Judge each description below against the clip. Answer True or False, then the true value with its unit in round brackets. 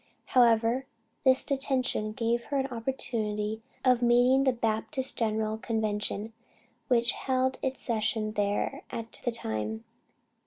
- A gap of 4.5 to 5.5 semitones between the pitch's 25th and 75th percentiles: False (3.1 semitones)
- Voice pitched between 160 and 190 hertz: False (230 Hz)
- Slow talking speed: True (120 wpm)